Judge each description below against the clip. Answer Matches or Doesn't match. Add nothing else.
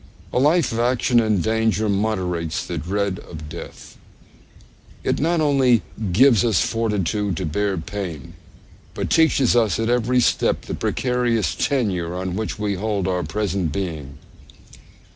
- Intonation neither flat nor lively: Matches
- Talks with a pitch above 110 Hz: Doesn't match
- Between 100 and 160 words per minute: Matches